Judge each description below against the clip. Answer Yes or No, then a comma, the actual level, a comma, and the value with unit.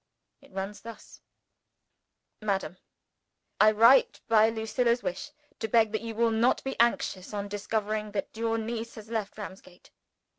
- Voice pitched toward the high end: Yes, high, 220 Hz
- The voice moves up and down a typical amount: No, narrow, 1.9 semitones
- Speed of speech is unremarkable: Yes, average, 145 wpm